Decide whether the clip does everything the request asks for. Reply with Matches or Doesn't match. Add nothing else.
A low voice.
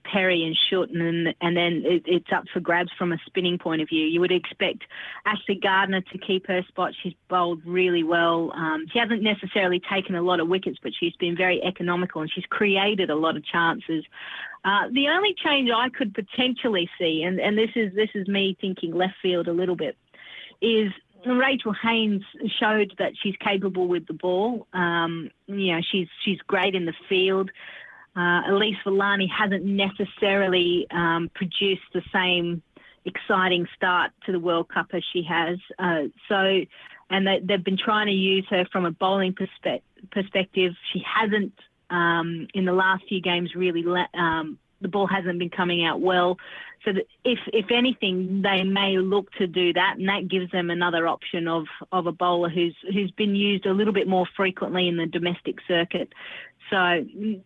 Doesn't match